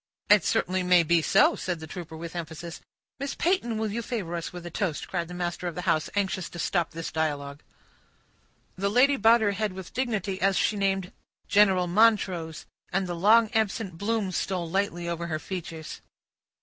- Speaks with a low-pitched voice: No, medium, 185 Hz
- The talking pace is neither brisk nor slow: Yes, average, 190 wpm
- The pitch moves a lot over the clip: No, average, 3.4 semitones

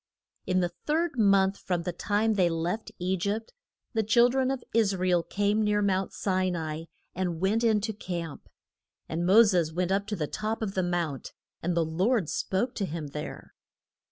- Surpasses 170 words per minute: Yes, average, 200 wpm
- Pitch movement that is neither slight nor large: Yes, average, 3.6 semitones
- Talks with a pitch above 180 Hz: Yes, high, 190 Hz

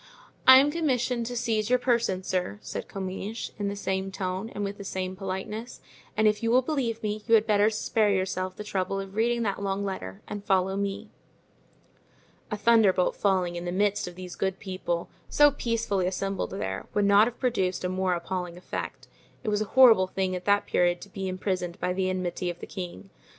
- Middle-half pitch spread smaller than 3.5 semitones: Yes, average, 2.9 semitones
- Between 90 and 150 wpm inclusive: No, fast, 205 wpm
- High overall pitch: Yes, high, 195 Hz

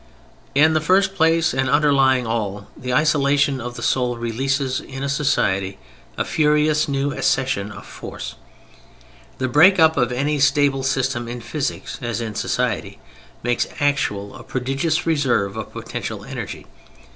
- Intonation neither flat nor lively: Yes, average, 3.6 semitones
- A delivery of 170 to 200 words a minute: No, average, 145 wpm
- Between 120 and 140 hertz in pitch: Yes, low, 135 Hz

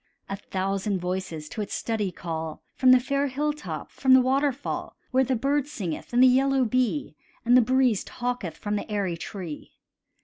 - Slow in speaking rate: No, average, 175 wpm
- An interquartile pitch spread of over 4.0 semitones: Yes, wide, 5.6 semitones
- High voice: Yes, high, 240 Hz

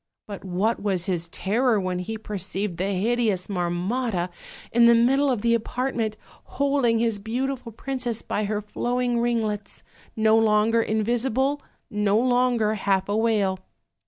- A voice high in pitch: Yes, high, 220 Hz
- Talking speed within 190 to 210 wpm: No, average, 145 wpm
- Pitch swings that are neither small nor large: Yes, average, 3.1 semitones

